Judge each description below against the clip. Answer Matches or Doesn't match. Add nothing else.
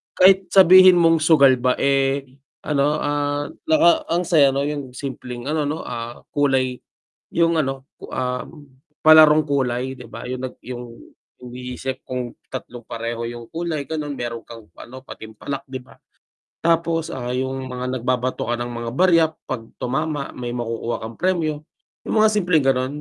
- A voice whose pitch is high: Doesn't match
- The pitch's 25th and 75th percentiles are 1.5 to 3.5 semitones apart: Doesn't match